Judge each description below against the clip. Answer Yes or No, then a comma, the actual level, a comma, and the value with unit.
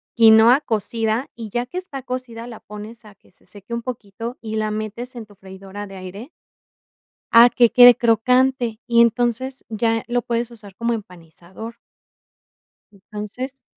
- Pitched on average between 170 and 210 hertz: No, high, 230 Hz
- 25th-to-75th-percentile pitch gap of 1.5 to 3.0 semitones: Yes, narrow, 2.5 semitones